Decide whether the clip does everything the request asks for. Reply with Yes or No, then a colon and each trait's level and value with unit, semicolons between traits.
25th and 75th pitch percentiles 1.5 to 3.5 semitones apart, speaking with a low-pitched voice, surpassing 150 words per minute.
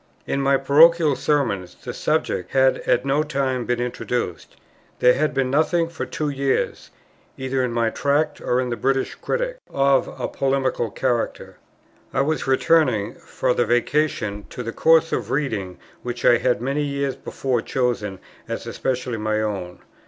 Yes: average, 2.9 semitones; low, 130 Hz; average, 160 wpm